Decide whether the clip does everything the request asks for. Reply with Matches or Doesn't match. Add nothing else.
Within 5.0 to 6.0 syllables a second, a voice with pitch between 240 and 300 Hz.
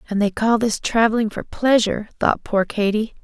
Doesn't match